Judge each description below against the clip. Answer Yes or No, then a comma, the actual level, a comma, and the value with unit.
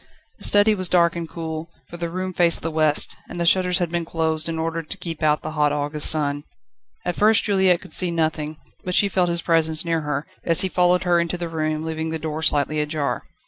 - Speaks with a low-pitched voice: No, medium, 165 Hz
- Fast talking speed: Yes, fast, 230 wpm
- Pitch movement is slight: Yes, narrow, 2.2 semitones